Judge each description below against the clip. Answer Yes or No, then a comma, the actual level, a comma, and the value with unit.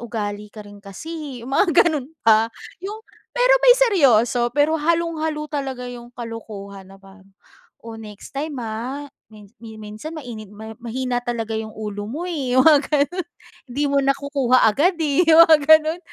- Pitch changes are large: Yes, wide, 6.0 semitones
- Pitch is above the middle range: Yes, very high, 255 Hz